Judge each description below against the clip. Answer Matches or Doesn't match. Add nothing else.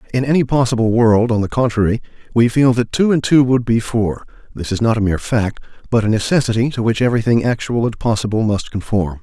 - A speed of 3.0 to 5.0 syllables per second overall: Doesn't match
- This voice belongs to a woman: Doesn't match